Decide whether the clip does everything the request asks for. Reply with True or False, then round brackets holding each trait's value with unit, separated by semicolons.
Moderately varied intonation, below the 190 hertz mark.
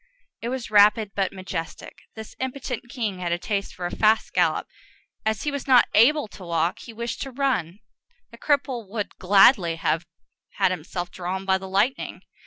False (4.8 semitones; 205 Hz)